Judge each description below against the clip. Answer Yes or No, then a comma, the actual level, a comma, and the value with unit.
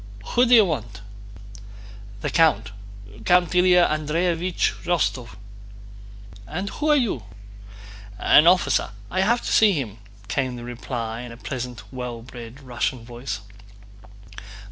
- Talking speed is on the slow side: Yes, slow, 120 wpm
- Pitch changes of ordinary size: No, wide, 7.3 semitones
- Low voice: Yes, low, 130 Hz